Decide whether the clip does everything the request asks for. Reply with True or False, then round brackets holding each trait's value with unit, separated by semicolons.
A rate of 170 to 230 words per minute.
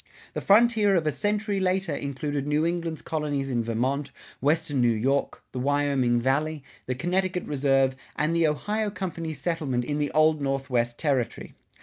False (155 wpm)